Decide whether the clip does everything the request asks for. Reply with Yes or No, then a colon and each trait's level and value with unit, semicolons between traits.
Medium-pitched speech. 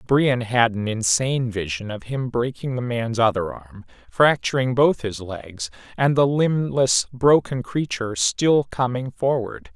No: low, 120 Hz